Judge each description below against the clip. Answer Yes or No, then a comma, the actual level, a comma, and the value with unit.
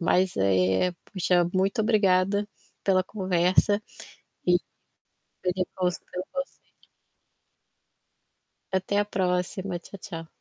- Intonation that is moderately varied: No, narrow, 2.0 semitones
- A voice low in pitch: No, medium, 185 Hz